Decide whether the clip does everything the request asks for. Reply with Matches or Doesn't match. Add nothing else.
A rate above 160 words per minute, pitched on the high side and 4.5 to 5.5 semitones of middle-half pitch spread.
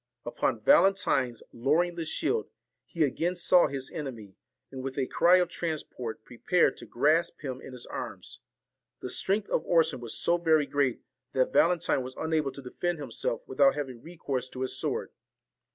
Doesn't match